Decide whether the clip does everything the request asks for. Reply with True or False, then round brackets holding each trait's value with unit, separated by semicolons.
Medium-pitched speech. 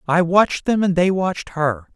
True (175 Hz)